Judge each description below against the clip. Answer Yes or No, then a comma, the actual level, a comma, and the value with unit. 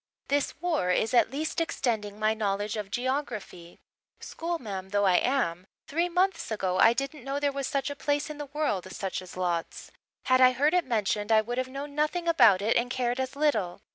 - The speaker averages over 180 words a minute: Yes, average, 200 wpm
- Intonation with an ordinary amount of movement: No, wide, 5.9 semitones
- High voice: Yes, very high, 250 Hz